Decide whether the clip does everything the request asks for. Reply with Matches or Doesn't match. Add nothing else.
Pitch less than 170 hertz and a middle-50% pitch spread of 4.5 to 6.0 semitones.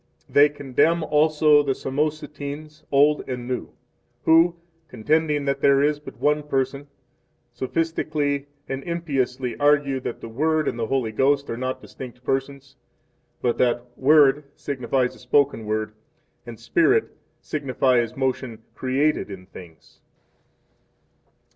Doesn't match